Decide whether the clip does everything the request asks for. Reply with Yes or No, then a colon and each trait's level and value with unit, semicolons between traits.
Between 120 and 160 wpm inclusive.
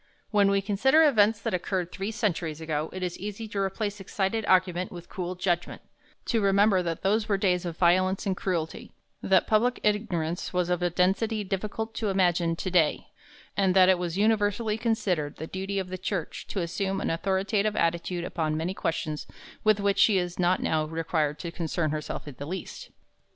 No: average, 190 wpm